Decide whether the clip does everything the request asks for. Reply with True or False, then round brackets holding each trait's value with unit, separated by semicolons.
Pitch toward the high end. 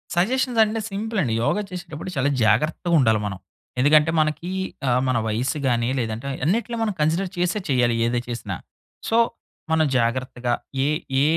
False (150 Hz)